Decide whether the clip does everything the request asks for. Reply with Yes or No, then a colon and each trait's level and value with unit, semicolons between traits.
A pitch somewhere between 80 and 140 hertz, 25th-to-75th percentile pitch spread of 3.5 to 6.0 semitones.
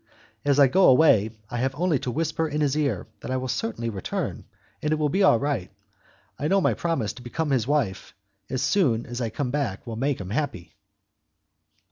Yes: low, 135 Hz; average, 4.5 semitones